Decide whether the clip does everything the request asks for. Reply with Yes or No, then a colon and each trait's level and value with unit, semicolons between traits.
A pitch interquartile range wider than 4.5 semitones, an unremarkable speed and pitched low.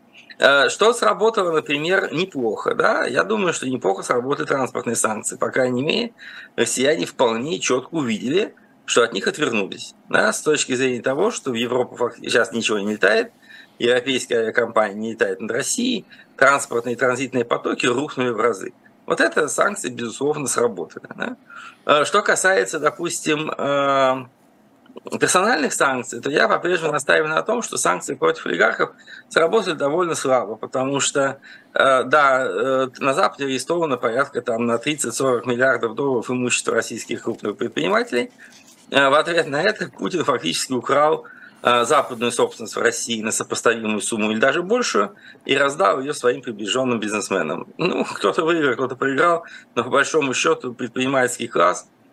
Yes: average, 5.1 semitones; average, 140 wpm; low, 130 Hz